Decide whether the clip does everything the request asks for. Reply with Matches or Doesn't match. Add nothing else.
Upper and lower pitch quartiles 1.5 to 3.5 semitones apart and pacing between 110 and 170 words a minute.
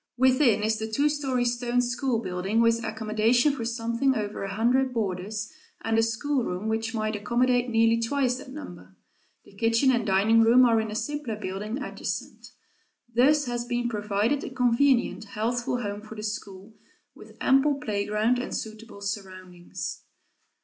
Matches